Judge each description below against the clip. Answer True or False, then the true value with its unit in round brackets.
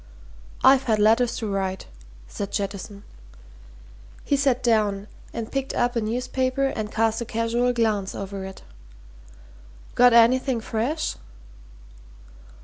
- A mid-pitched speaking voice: False (230 Hz)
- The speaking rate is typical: False (120 wpm)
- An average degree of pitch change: True (3.2 semitones)